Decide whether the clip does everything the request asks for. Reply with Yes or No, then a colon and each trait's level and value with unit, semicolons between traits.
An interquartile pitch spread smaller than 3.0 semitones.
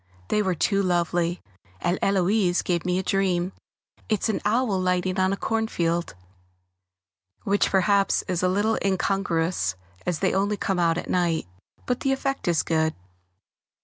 Yes: narrow, 2.4 semitones